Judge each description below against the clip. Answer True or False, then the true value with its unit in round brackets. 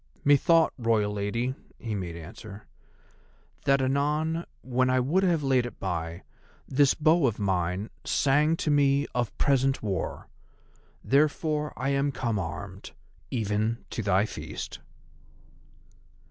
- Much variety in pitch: True (5.7 semitones)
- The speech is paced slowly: True (120 wpm)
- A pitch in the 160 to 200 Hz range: False (125 Hz)